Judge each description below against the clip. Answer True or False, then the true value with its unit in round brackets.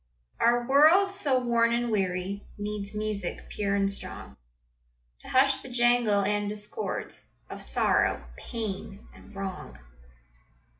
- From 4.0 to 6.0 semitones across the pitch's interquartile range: False (3.3 semitones)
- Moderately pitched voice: False (215 Hz)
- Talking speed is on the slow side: True (120 wpm)